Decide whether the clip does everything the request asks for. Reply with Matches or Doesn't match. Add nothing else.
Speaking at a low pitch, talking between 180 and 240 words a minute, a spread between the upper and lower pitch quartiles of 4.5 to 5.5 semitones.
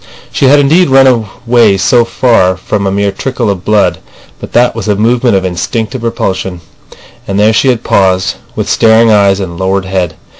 Doesn't match